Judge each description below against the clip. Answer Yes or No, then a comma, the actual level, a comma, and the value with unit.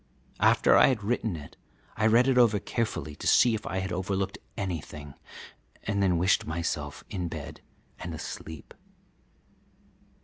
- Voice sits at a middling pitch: No, very low, 95 Hz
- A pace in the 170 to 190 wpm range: No, average, 145 wpm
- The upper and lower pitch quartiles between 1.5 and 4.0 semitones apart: No, average, 4.9 semitones